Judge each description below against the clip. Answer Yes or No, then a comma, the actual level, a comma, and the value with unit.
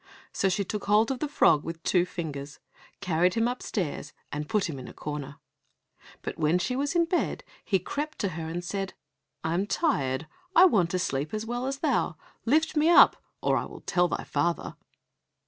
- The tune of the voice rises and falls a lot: Yes, wide, 7.6 semitones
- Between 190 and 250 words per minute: Yes, average, 200 wpm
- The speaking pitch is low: No, medium, 185 Hz